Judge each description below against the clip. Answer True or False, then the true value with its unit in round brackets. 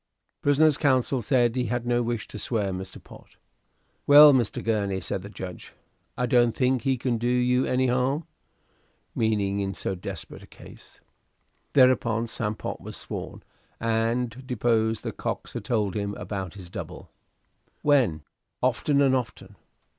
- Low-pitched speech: True (120 Hz)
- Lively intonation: False (3.6 semitones)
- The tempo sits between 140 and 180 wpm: True (155 wpm)